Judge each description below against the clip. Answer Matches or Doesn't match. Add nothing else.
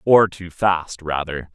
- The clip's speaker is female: Doesn't match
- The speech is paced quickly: Doesn't match